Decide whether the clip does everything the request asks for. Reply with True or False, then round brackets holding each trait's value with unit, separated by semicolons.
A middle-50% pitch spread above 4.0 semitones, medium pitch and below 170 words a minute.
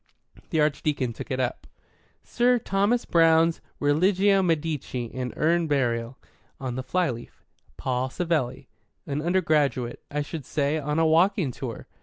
True (4.7 semitones; 150 Hz; 135 wpm)